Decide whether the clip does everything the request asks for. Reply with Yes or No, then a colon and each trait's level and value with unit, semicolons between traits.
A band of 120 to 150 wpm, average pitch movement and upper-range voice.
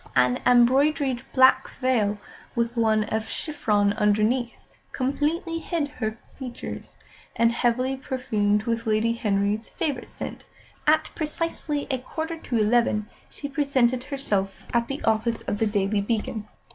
Yes: slow, 135 wpm; average, 4.2 semitones; high, 235 Hz